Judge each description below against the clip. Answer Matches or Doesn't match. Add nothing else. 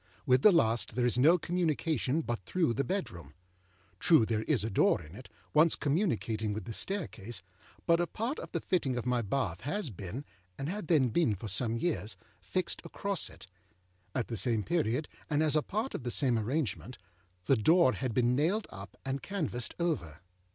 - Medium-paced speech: Matches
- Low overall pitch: Matches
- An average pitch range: Doesn't match